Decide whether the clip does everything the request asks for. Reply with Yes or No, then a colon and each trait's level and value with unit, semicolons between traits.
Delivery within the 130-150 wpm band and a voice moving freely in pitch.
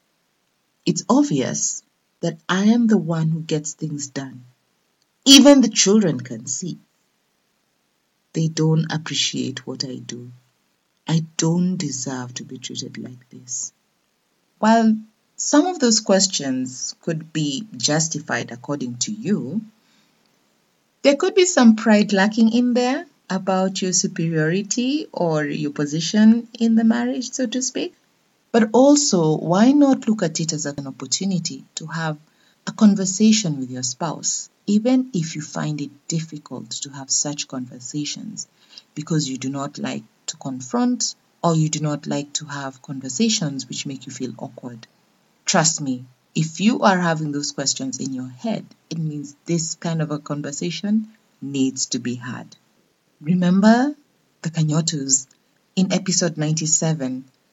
Yes: average, 140 wpm; wide, 7.3 semitones